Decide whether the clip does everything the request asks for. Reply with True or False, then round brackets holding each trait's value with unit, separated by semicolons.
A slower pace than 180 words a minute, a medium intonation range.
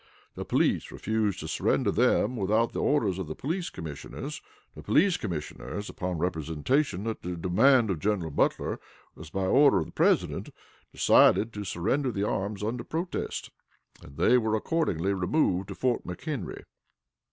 False (155 wpm; 5.9 semitones)